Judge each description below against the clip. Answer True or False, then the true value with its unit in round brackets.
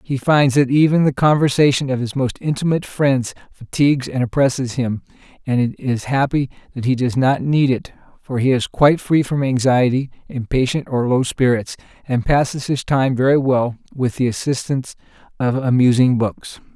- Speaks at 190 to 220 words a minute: False (170 wpm)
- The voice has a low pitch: True (130 Hz)